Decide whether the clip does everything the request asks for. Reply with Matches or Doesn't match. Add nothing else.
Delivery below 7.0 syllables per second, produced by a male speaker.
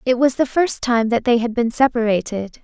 Doesn't match